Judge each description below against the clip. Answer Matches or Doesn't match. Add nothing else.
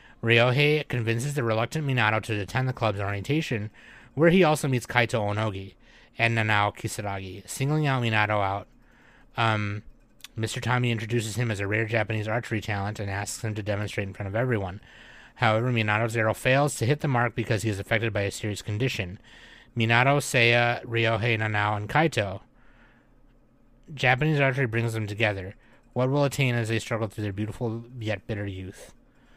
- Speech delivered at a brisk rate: Doesn't match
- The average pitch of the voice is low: Matches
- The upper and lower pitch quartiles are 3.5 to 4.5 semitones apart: Doesn't match